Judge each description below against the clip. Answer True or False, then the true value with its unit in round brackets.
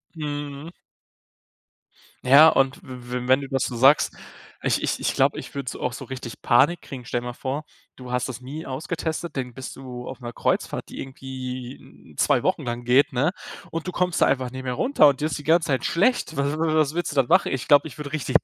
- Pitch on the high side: False (135 Hz)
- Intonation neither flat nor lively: True (3.2 semitones)